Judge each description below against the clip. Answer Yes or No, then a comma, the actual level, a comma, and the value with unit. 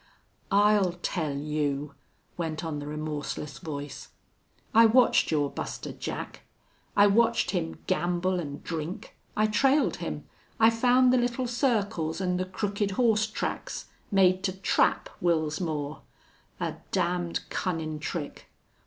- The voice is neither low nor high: Yes, medium, 180 Hz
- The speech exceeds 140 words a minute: No, slow, 135 wpm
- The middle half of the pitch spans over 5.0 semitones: Yes, wide, 5.4 semitones